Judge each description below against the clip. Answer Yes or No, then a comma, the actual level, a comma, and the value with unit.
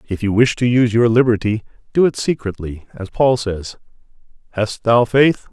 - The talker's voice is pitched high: No, low, 115 Hz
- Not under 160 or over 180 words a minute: Yes, average, 175 wpm